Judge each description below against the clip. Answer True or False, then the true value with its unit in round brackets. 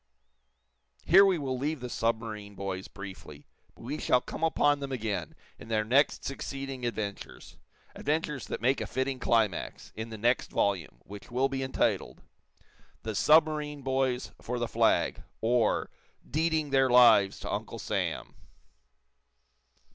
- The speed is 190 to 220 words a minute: False (140 wpm)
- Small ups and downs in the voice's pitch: False (4.1 semitones)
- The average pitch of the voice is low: True (125 Hz)